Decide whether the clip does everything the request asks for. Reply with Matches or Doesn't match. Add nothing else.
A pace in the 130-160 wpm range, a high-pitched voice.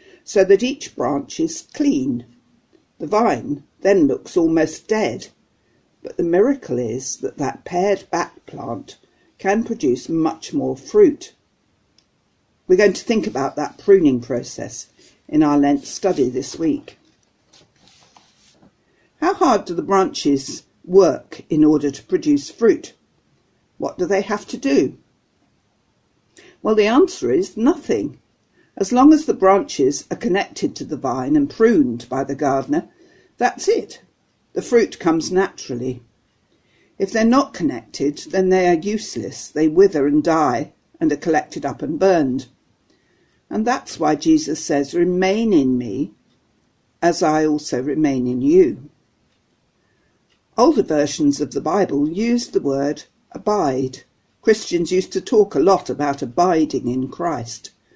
Matches